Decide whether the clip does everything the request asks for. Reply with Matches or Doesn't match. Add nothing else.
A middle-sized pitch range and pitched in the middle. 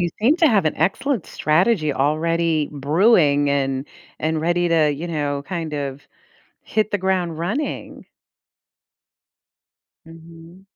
Matches